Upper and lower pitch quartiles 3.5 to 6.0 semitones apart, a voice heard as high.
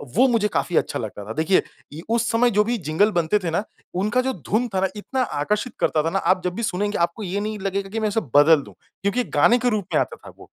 Yes: average, 4.7 semitones; high, 205 Hz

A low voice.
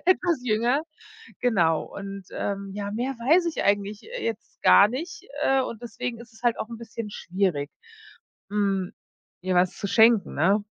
No: high, 220 Hz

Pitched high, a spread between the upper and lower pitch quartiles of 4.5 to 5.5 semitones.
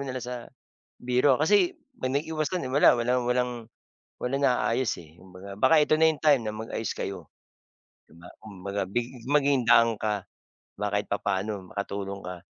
No: low, 115 Hz; average, 5.2 semitones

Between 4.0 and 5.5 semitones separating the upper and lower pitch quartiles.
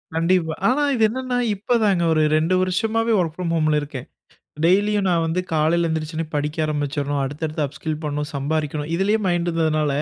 No: average, 3.5 semitones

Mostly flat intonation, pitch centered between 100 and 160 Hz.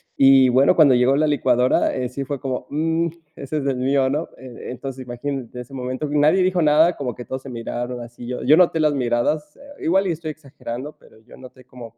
No: average, 3.3 semitones; low, 135 Hz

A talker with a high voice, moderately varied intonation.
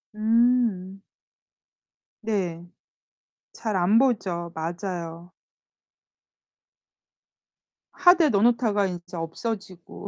Yes: high, 195 Hz; average, 4.7 semitones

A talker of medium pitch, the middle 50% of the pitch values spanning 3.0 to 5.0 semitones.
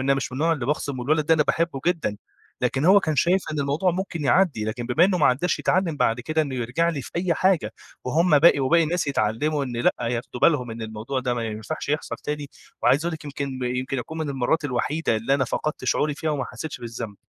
Yes: medium, 145 Hz; average, 4.4 semitones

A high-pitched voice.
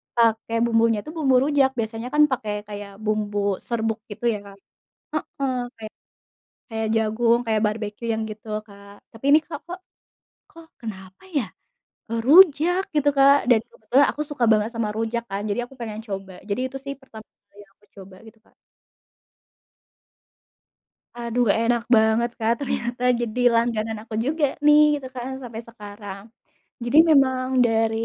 Yes: high, 230 Hz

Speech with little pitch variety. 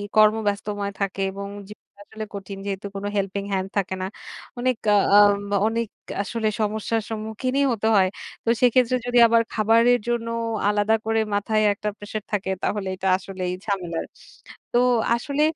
Yes: narrow, 2.3 semitones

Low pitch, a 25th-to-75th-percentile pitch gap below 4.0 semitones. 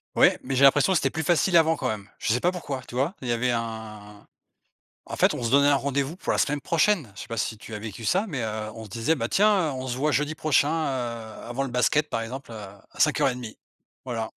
No: low, 130 Hz; average, 5.0 semitones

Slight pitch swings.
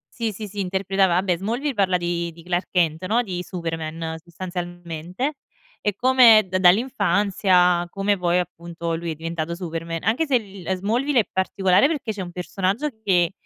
No: average, 3.2 semitones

